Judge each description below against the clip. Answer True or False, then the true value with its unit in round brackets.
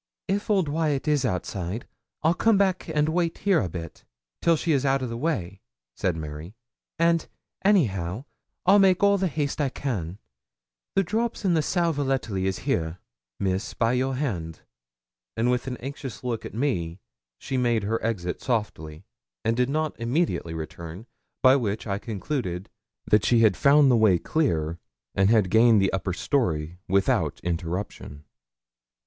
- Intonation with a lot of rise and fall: True (8.2 semitones)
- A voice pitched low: True (120 Hz)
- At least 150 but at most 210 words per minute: True (160 wpm)